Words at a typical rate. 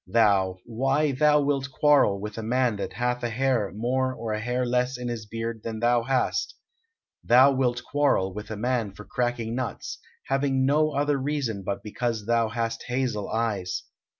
Yes: average, 180 wpm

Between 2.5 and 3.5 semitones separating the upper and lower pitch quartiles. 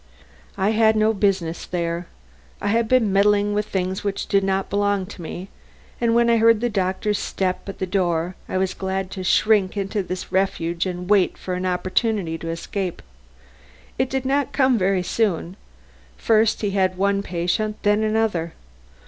Yes: average, 2.8 semitones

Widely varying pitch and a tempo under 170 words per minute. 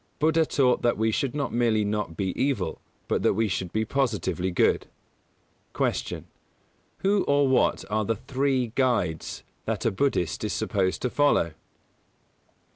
Yes: wide, 5.7 semitones; average, 155 wpm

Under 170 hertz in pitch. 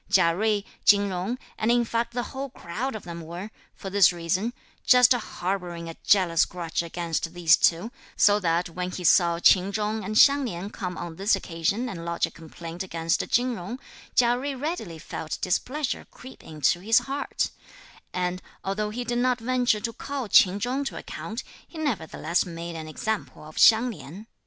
No: high, 195 Hz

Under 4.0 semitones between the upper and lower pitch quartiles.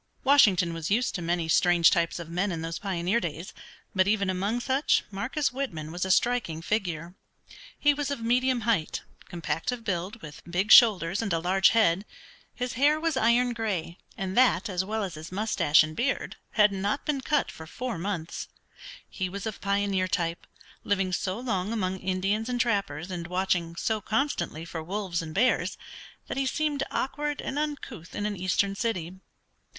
No: average, 5.3 semitones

